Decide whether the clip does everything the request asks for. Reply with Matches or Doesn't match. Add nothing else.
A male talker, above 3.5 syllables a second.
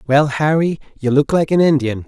Matches